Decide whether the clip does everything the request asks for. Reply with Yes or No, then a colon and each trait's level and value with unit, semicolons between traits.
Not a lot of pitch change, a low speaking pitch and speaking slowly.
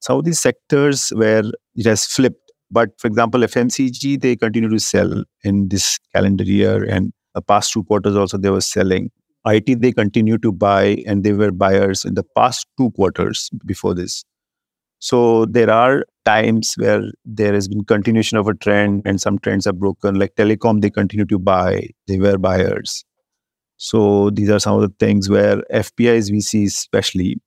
No: narrow, 2.3 semitones; low, 105 Hz; average, 180 wpm